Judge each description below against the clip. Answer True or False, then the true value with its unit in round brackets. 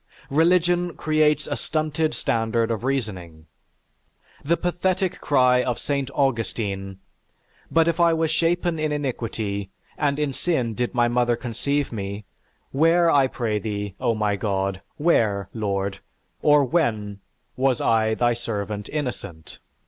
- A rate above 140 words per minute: False (135 wpm)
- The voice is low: True (125 Hz)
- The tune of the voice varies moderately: False (6.4 semitones)